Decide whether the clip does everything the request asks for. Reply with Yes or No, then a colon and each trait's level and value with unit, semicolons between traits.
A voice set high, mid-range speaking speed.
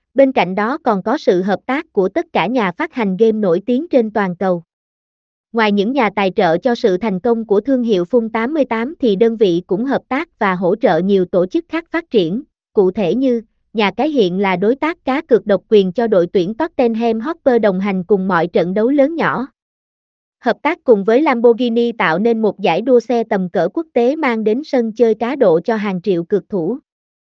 Yes: high, 230 Hz; average, 225 wpm